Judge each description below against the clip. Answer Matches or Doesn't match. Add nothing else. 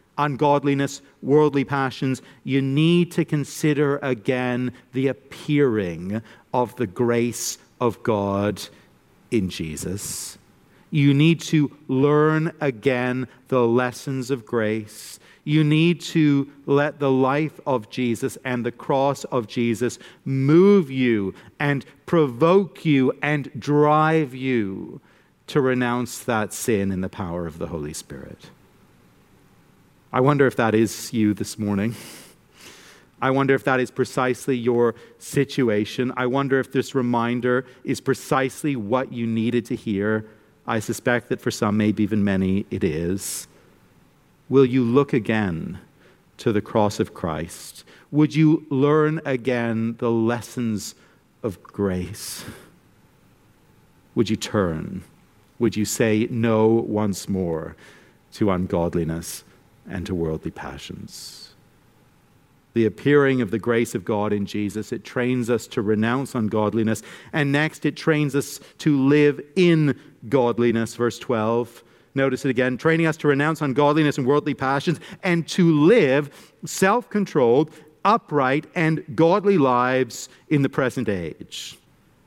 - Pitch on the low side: Matches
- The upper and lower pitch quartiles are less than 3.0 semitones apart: Doesn't match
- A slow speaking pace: Matches